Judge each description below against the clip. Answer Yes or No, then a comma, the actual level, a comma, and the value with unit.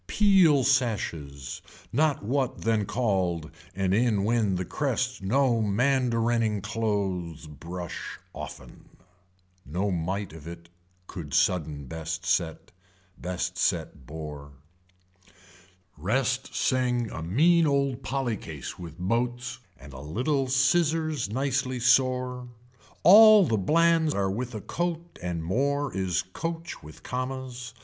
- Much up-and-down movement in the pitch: Yes, wide, 7.1 semitones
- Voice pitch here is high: No, low, 115 Hz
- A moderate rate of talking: No, slow, 120 wpm